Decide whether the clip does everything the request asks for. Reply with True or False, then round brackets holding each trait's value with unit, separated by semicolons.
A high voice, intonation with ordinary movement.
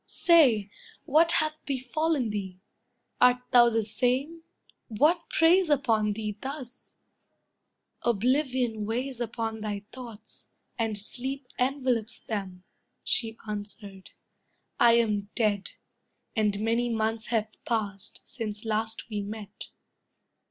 True (230 Hz; 3.5 semitones)